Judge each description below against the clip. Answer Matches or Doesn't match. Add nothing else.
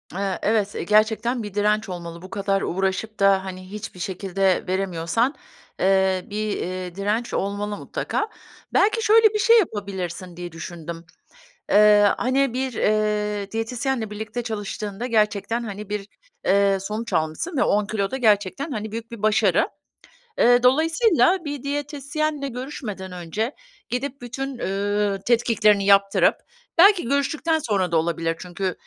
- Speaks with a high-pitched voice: Matches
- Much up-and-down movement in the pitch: Doesn't match